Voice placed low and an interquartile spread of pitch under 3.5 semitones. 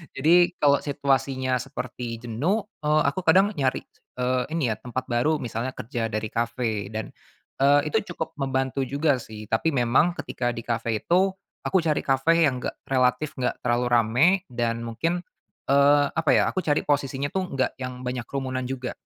No: low, 130 Hz; average, 3.8 semitones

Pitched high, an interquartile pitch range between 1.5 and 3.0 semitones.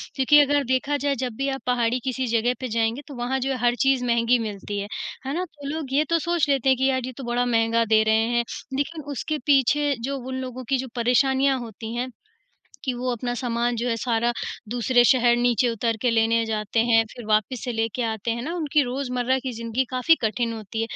Yes: high, 245 Hz; narrow, 2.6 semitones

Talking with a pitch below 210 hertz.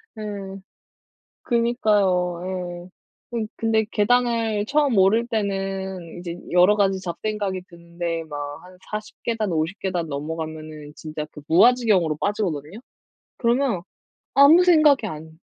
Yes: high, 190 Hz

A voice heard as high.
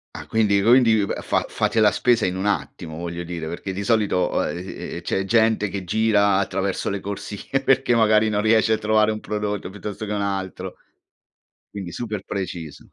No: low, 105 Hz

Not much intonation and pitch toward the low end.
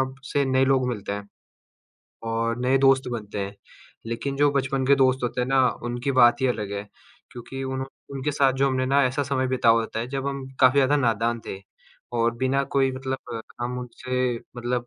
Yes: narrow, 2.2 semitones; low, 130 Hz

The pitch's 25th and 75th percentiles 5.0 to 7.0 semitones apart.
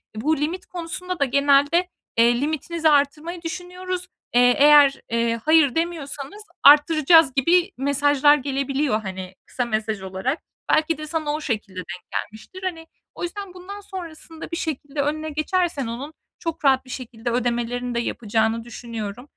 Yes: average, 5.3 semitones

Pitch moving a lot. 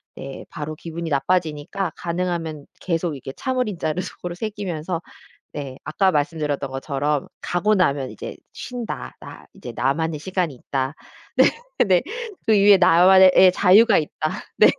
No: average, 4.2 semitones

